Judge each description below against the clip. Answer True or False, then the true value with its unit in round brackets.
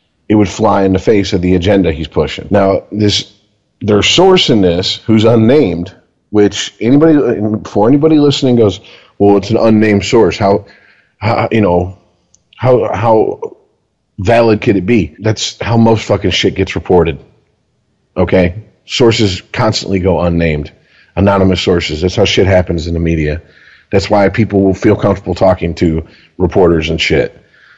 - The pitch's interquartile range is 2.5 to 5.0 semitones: True (3.5 semitones)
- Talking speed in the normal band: True (155 wpm)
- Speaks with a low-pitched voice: True (100 Hz)